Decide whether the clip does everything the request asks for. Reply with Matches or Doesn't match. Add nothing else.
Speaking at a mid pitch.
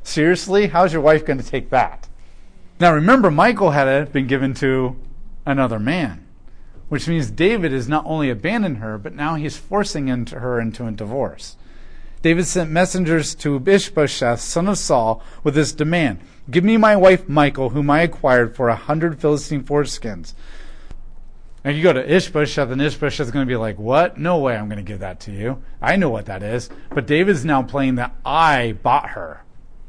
Matches